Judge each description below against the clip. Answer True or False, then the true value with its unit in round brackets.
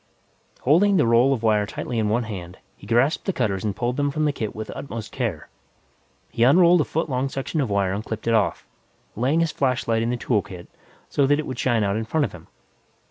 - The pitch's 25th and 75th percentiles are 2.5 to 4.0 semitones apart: False (4.6 semitones)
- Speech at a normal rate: False (235 wpm)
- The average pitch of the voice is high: False (120 Hz)